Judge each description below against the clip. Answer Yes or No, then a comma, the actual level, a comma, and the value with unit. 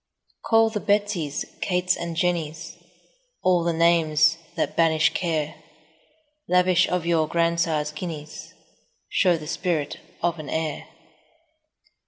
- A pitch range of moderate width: No, narrow, 2.3 semitones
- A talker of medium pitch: Yes, medium, 170 Hz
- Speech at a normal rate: No, slow, 120 wpm